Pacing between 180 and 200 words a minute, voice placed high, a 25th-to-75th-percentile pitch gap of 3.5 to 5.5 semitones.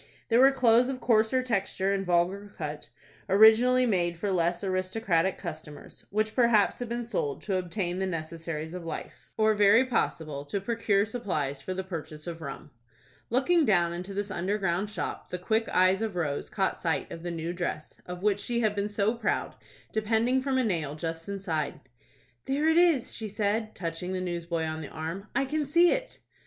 Yes: average, 190 wpm; high, 195 Hz; average, 4.8 semitones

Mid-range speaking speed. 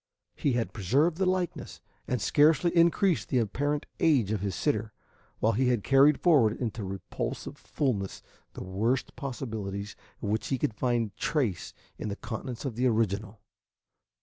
Yes: average, 155 wpm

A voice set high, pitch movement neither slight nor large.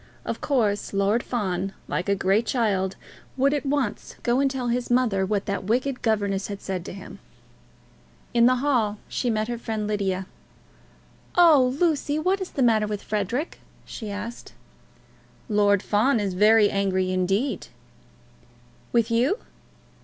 Yes: high, 220 Hz; average, 4.1 semitones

